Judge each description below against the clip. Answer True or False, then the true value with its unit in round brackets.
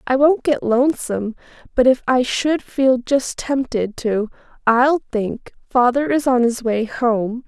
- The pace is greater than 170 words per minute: False (160 wpm)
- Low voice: False (250 Hz)